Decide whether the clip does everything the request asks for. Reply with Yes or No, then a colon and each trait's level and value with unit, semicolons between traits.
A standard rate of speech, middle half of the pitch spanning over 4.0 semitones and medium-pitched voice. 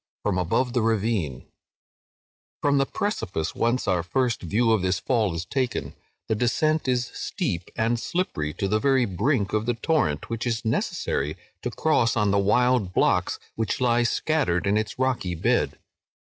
No: average, 170 wpm; average, 4.8 semitones; low, 115 Hz